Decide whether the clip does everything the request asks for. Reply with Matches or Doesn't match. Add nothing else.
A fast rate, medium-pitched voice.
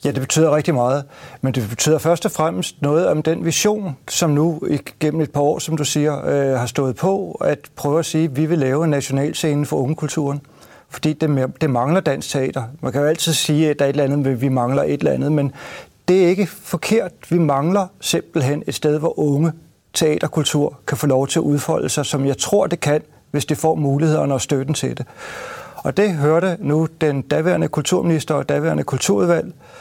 Doesn't match